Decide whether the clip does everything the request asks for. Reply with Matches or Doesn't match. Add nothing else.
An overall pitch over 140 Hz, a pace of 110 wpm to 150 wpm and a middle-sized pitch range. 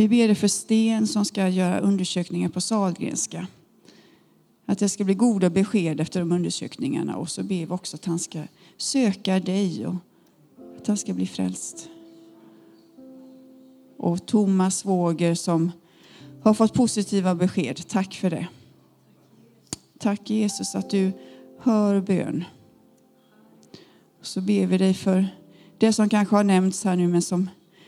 Matches